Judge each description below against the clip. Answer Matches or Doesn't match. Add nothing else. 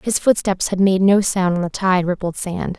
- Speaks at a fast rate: Matches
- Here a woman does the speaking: Matches